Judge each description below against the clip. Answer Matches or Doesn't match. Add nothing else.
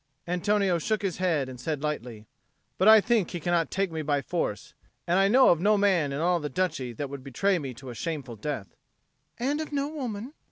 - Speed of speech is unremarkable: Doesn't match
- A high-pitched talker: Doesn't match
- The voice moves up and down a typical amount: Doesn't match